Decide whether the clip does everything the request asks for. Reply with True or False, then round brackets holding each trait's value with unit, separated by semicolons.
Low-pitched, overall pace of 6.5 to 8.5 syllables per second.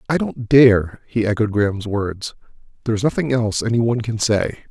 False (115 Hz; 5.5 syllables/s)